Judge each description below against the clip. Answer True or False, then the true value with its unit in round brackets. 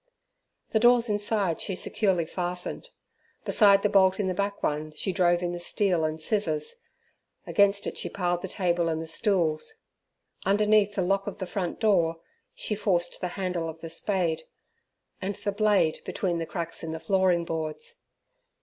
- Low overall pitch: False (185 Hz)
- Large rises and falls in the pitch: False (3.3 semitones)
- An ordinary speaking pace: True (170 wpm)